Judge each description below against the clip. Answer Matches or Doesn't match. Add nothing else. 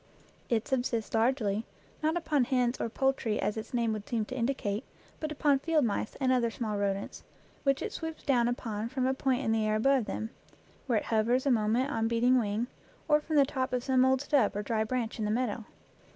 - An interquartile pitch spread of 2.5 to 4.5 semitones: Matches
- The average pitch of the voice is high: Matches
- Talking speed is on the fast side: Matches